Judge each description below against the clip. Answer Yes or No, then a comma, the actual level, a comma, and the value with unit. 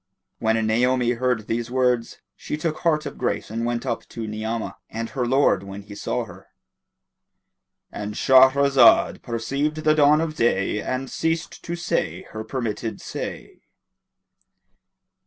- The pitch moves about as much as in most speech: Yes, average, 4.0 semitones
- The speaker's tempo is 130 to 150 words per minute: Yes, average, 140 wpm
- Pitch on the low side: Yes, low, 125 Hz